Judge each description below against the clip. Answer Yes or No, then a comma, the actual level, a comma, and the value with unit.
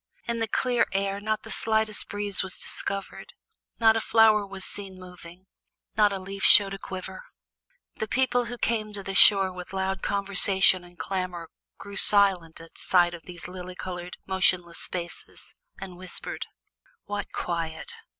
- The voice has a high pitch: Yes, high, 195 Hz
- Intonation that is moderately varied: No, narrow, 2.3 semitones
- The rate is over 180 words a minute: No, average, 160 wpm